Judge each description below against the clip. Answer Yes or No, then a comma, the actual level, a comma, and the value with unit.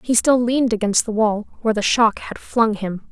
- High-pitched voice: Yes, high, 220 Hz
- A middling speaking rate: No, fast, 230 wpm